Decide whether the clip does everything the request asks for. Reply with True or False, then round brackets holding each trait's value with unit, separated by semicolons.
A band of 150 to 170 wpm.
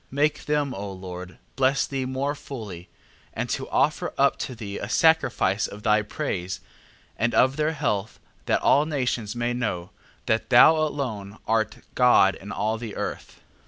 True (160 wpm)